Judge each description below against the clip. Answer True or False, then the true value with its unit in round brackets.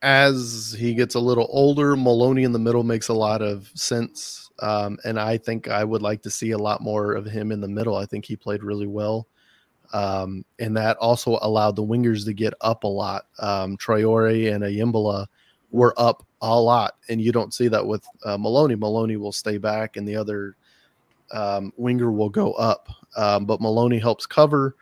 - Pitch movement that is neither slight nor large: False (2.1 semitones)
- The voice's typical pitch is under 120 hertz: True (110 Hz)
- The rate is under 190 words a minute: False (200 wpm)